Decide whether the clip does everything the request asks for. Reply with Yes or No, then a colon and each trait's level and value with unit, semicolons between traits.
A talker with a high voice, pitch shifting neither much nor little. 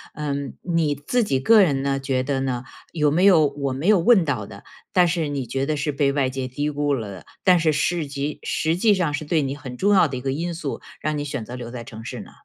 No: medium, 145 Hz; average, 3.6 semitones